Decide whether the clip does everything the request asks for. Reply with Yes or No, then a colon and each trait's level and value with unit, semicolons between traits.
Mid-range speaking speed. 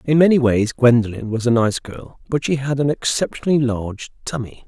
Yes: average, 190 wpm